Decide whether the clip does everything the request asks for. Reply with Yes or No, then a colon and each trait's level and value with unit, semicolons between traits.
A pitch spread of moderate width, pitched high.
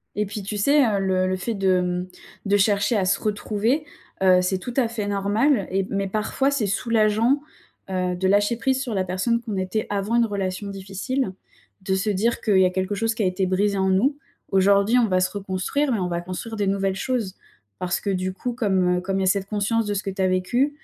Yes: average, 3.1 semitones; high, 200 Hz